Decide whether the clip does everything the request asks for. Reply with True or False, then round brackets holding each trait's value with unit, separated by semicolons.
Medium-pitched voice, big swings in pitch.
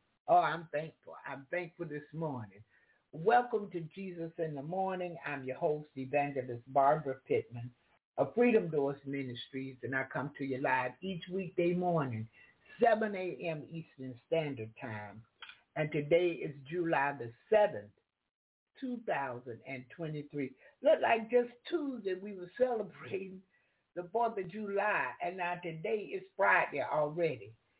True (165 Hz; 6.2 semitones)